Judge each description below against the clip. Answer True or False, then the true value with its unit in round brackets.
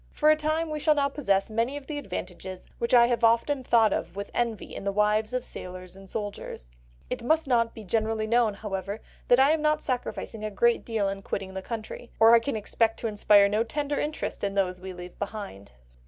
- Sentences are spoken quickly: True (220 wpm)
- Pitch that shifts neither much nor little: True (4.0 semitones)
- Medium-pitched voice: False (225 Hz)